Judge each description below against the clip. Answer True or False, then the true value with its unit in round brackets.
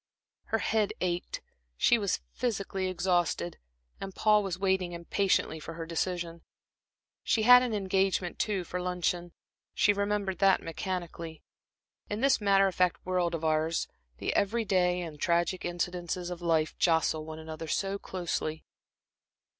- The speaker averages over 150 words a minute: False (145 wpm)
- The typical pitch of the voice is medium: True (180 Hz)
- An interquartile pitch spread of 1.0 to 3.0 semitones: True (2.6 semitones)